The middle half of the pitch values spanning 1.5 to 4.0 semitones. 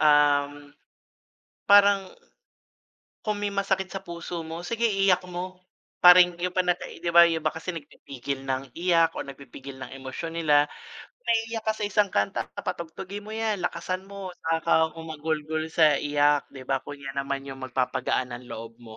No: average, 5.0 semitones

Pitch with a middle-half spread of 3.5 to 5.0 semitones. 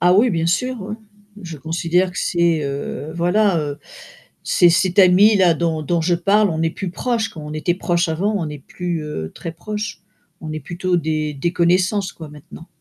No: average, 2.8 semitones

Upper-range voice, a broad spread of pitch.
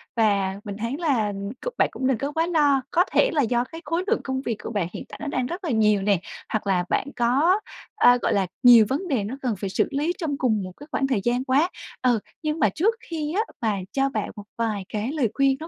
Yes: very high, 255 Hz; wide, 5.8 semitones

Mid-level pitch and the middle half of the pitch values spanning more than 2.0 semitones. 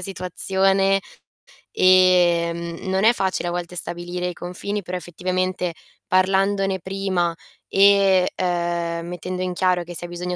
No: medium, 180 Hz; narrow, 1.5 semitones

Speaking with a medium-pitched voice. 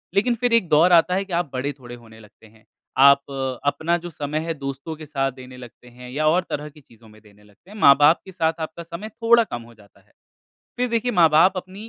Yes: medium, 150 Hz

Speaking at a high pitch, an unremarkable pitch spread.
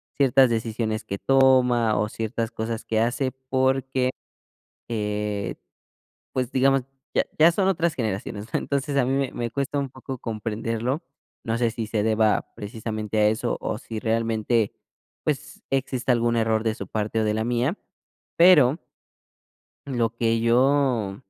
No: low, 115 Hz; average, 3.2 semitones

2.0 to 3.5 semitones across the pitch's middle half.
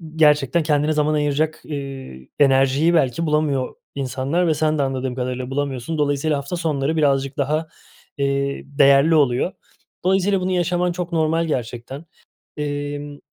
Yes: average, 2.7 semitones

